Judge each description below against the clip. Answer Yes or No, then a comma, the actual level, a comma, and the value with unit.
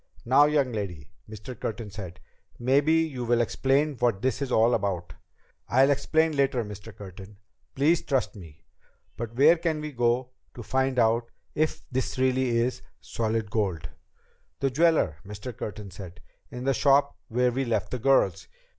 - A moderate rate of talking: Yes, average, 160 wpm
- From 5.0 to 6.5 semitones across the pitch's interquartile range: No, average, 4.6 semitones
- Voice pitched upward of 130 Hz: No, low, 120 Hz